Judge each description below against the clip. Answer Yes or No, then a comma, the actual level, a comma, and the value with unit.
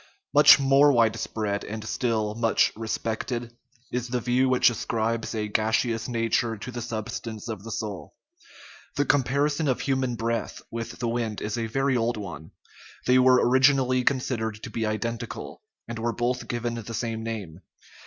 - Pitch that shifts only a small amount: Yes, narrow, 2.2 semitones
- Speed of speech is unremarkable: Yes, average, 165 wpm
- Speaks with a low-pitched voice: Yes, low, 115 Hz